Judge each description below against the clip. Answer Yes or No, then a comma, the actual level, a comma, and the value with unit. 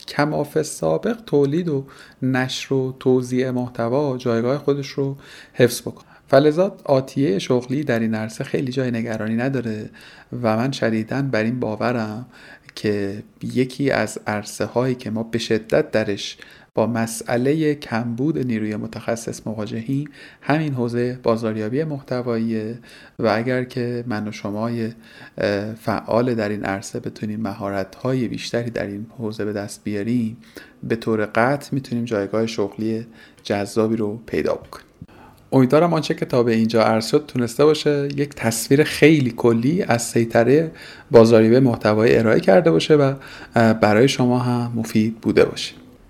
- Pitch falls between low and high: No, low, 120 Hz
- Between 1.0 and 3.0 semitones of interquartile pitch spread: No, average, 3.4 semitones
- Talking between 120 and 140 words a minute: Yes, average, 135 wpm